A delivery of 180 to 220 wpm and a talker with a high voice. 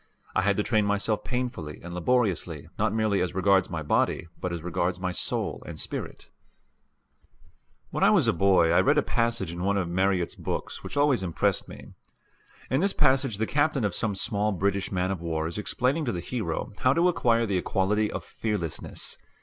No: average, 190 wpm; low, 100 Hz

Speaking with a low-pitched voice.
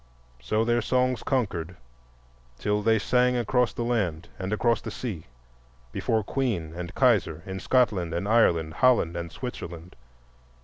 Yes: low, 105 Hz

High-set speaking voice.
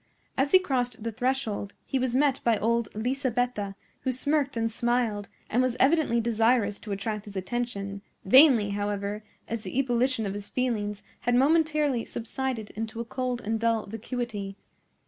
Yes: high, 235 Hz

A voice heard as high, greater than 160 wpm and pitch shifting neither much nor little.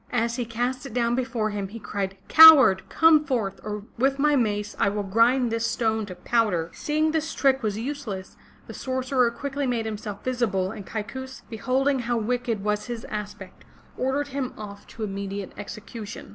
Yes: high, 230 Hz; average, 180 wpm; average, 3.9 semitones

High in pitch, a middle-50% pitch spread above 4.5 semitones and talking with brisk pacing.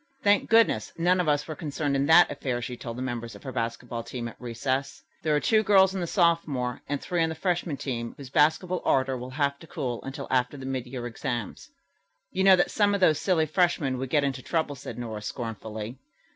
No: medium, 140 Hz; average, 5.1 semitones; fast, 225 wpm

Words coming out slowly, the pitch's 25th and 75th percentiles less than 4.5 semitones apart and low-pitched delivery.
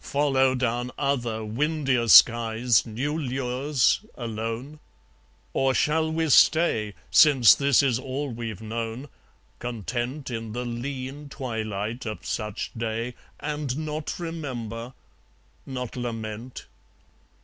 Yes: slow, 105 wpm; average, 3.6 semitones; low, 125 Hz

